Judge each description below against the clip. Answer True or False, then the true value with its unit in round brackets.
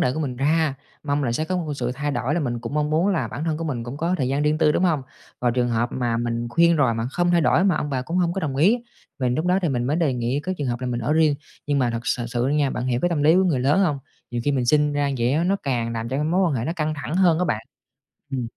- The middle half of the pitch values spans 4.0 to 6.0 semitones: True (4.6 semitones)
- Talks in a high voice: False (145 Hz)